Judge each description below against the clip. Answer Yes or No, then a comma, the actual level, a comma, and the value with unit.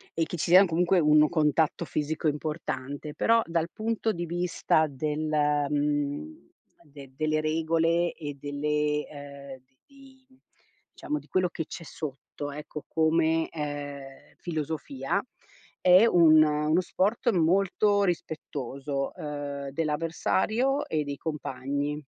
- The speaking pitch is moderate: Yes, medium, 155 Hz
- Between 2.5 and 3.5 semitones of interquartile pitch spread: Yes, average, 2.8 semitones